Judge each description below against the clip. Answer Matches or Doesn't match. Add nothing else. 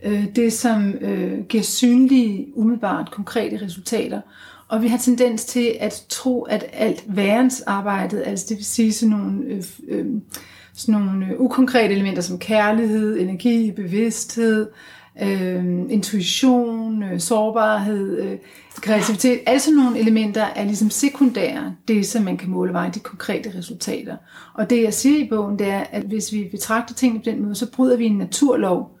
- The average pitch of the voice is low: Doesn't match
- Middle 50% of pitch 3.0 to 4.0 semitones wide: Doesn't match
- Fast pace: Doesn't match